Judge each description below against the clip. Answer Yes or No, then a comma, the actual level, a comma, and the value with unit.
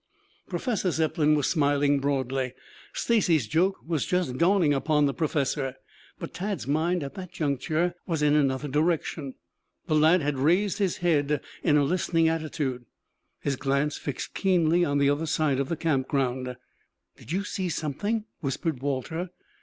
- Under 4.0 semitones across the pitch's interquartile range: Yes, average, 3.6 semitones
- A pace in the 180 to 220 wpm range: No, average, 155 wpm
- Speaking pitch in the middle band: Yes, medium, 150 Hz